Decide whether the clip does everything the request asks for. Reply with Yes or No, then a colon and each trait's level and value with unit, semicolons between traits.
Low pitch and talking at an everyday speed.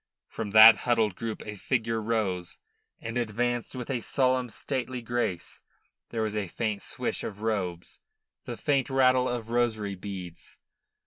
Yes: low, 115 Hz; average, 145 wpm